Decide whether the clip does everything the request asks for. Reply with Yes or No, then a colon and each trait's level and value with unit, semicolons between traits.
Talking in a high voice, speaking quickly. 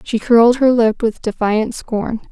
No: high, 230 Hz; average, 180 wpm